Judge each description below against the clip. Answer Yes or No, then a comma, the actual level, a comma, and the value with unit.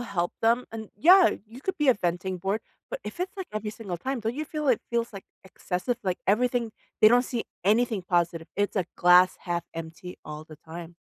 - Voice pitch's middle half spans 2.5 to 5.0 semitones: No, wide, 5.6 semitones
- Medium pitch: No, high, 210 Hz